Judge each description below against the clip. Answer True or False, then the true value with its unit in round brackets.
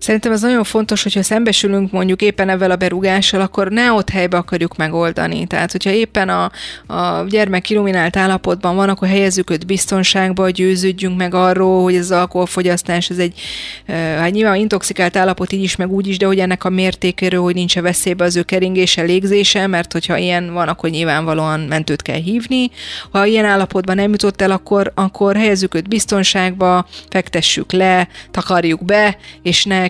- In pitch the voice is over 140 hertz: True (185 Hz)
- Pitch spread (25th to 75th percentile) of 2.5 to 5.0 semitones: False (1.8 semitones)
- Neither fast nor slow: False (175 wpm)